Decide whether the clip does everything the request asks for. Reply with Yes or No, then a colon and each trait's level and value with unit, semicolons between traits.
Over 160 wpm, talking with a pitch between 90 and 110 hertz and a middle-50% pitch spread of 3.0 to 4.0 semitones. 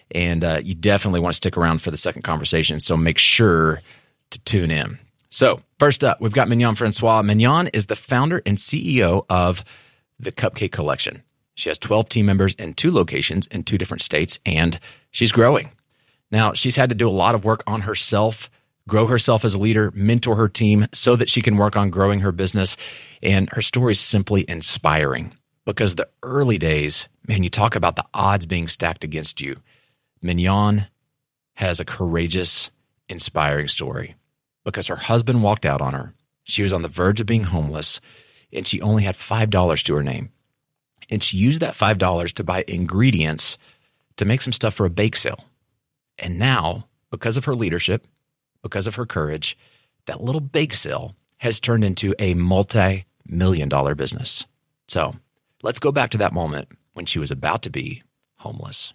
No: average, 180 wpm; low, 105 Hz; average, 5.0 semitones